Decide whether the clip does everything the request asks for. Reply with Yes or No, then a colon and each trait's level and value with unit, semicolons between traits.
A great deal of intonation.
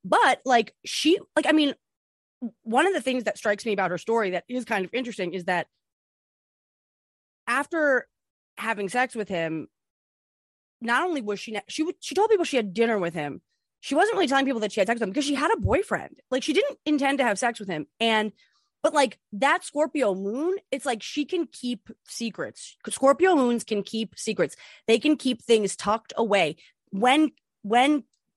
Yes: wide, 6.0 semitones